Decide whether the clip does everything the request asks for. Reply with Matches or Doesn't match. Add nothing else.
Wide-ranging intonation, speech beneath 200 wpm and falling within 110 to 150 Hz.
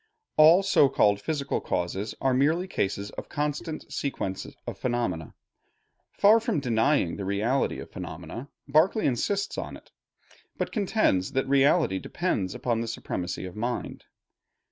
Matches